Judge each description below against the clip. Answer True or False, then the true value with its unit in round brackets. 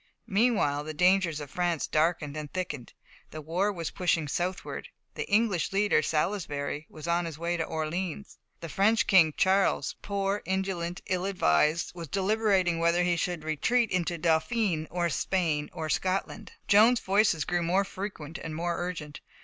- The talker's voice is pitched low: False (175 Hz)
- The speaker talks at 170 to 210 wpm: False (155 wpm)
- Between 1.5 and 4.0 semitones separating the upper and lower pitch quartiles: True (3.5 semitones)